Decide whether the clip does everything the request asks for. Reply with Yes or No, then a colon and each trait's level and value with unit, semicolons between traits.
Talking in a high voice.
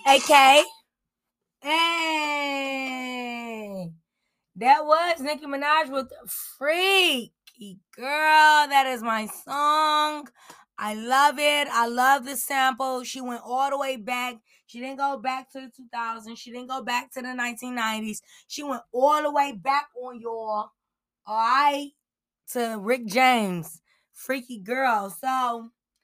Yes: very high, 260 Hz